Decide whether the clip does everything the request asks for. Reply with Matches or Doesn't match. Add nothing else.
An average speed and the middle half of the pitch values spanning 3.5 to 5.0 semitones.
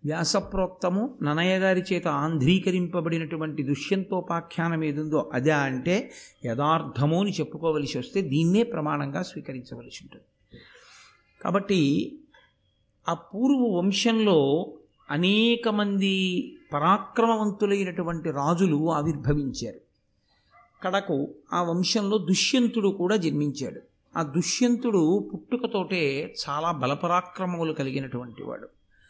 Matches